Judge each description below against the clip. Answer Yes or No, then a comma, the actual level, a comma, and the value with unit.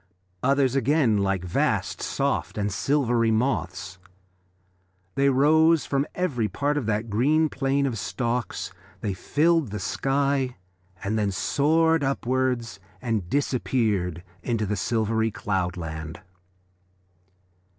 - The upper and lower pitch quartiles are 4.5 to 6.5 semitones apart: Yes, average, 5.3 semitones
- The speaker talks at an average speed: No, slow, 110 wpm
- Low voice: Yes, low, 120 Hz